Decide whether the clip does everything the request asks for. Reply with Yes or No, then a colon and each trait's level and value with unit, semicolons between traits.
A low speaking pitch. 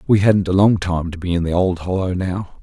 Yes: very low, 95 Hz